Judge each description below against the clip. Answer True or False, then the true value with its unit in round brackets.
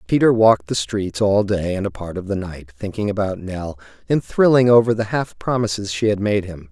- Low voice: True (100 Hz)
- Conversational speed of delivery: False (225 wpm)